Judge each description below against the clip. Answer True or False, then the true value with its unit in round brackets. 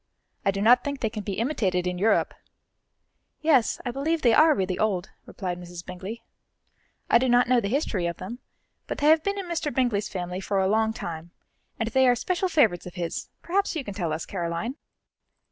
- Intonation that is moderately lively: False (6.5 semitones)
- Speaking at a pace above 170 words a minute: True (205 wpm)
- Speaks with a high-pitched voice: True (220 Hz)